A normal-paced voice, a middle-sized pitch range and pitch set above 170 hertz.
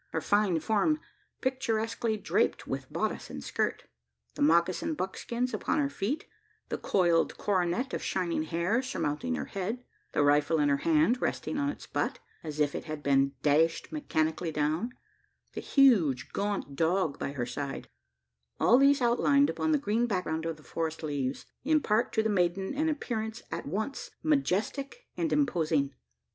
No: average, 155 wpm; wide, 8.2 semitones; high, 190 Hz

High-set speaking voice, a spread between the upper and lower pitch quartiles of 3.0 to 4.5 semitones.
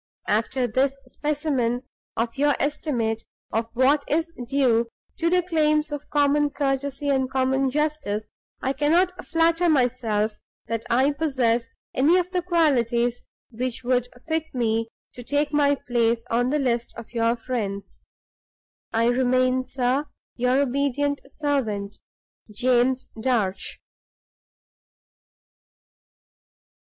Yes: very high, 260 Hz; average, 3.7 semitones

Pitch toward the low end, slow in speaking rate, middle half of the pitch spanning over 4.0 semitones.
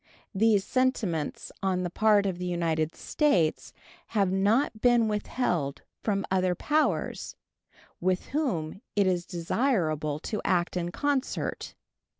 No: high, 190 Hz; slow, 125 wpm; average, 4.6 semitones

